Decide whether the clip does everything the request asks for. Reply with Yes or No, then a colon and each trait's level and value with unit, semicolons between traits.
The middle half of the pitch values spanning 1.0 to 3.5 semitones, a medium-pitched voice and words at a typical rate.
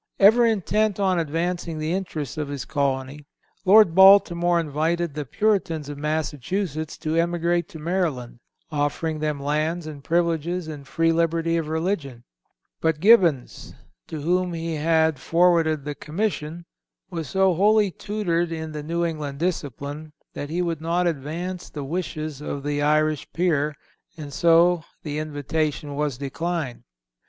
Yes: average, 2.7 semitones; medium, 160 Hz; average, 145 wpm